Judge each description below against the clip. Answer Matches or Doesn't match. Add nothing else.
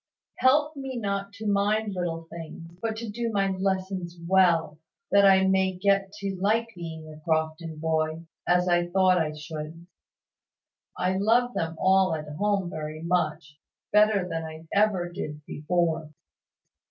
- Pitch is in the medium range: Matches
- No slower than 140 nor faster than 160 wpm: Matches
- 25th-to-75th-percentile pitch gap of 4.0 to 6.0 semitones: Doesn't match